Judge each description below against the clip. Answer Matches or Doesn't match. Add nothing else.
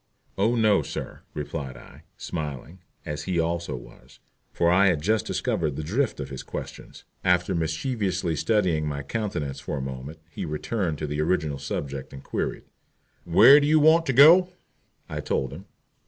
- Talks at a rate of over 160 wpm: Matches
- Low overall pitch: Matches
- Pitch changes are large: Matches